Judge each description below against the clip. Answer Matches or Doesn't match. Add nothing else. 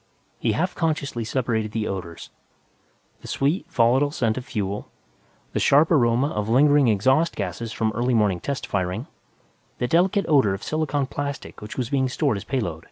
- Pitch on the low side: Matches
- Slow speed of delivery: Doesn't match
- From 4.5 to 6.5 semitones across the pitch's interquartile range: Matches